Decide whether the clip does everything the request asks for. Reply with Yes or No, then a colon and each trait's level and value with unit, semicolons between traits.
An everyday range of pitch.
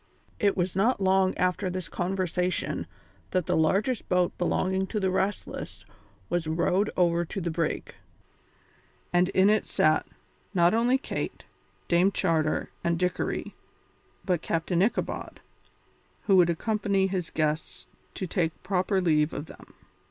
No: narrow, 2.2 semitones